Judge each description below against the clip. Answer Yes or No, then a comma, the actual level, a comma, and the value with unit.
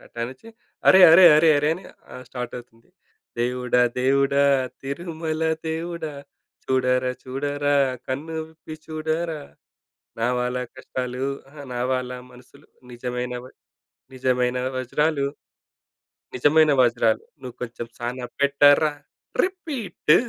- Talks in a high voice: No, low, 135 Hz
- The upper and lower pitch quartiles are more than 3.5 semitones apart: Yes, average, 4.0 semitones